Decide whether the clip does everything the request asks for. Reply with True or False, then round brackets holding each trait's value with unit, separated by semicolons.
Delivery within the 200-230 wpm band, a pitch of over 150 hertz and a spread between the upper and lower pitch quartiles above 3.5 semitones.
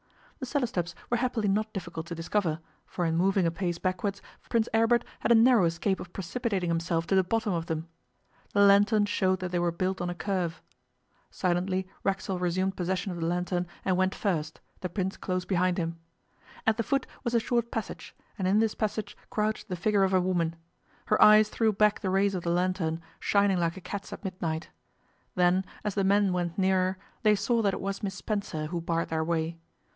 False (205 wpm; 190 Hz; 3.0 semitones)